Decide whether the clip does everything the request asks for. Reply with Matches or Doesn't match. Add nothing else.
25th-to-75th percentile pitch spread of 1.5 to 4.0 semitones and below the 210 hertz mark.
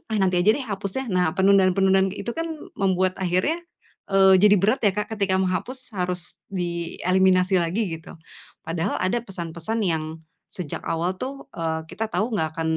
Matches